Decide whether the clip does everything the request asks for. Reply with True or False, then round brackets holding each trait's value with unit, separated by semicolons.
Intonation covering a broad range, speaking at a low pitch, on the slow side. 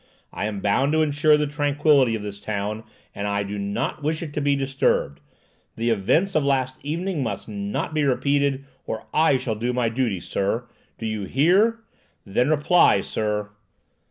False (5.8 semitones; 130 Hz; 175 wpm)